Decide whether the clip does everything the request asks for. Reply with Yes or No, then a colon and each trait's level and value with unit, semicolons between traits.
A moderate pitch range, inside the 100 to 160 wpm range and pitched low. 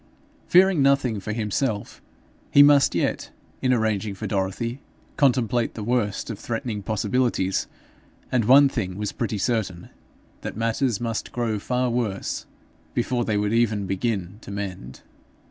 Yes: average, 3.4 semitones; average, 140 wpm; low, 115 Hz